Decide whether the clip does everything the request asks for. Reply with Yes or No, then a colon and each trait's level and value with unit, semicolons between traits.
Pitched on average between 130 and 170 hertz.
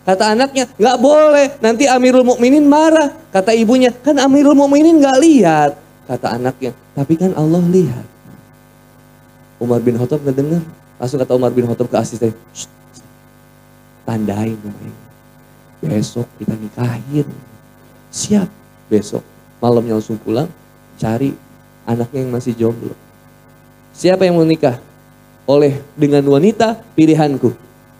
Yes: medium, 140 Hz